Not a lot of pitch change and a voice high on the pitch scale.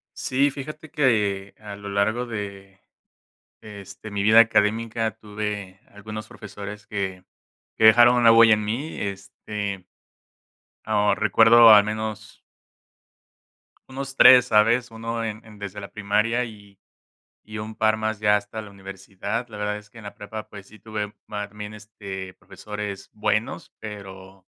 No: narrow, 1.8 semitones; low, 105 Hz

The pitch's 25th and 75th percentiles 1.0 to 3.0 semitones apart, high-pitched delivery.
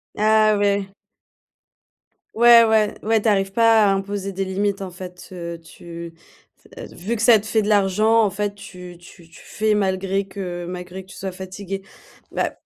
Yes: narrow, 2.5 semitones; high, 195 Hz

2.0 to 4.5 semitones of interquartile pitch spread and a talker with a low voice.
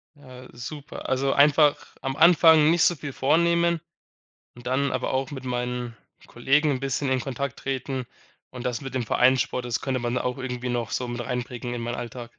Yes: narrow, 2.6 semitones; low, 130 Hz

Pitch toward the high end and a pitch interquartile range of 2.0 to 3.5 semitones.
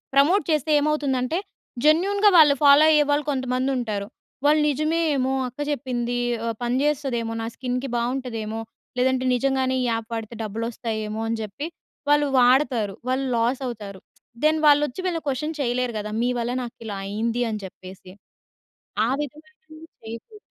No: very high, 255 Hz; average, 4.3 semitones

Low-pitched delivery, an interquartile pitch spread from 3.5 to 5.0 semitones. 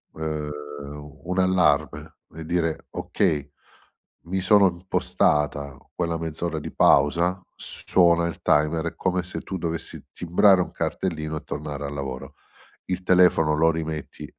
No: very low, 80 Hz; average, 2.9 semitones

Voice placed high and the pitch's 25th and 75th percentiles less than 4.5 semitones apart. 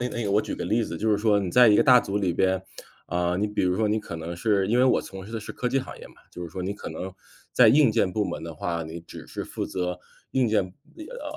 No: low, 100 Hz; average, 4.0 semitones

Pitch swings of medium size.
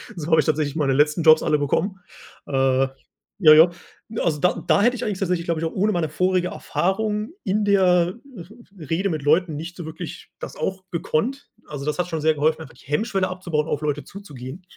Yes: average, 3.7 semitones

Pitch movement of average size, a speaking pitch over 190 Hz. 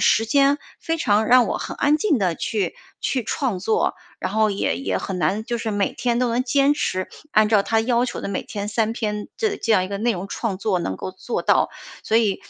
Yes: average, 3.6 semitones; high, 220 Hz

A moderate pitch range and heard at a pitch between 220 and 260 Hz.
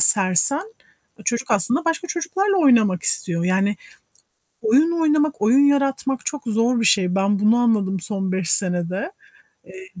No: wide, 6.9 semitones; high, 225 Hz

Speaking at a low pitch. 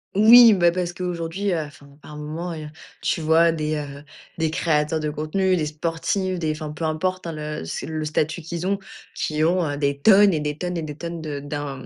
No: medium, 160 Hz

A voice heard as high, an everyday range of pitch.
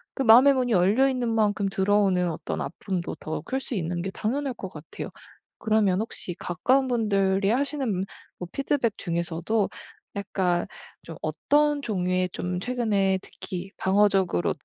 Yes: high, 200 Hz; average, 4.9 semitones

